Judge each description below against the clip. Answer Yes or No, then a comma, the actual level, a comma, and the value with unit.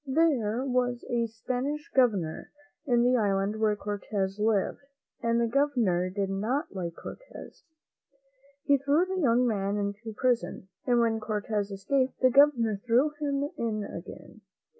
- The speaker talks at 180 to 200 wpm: No, average, 140 wpm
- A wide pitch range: No, average, 4.2 semitones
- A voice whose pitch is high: Yes, high, 230 Hz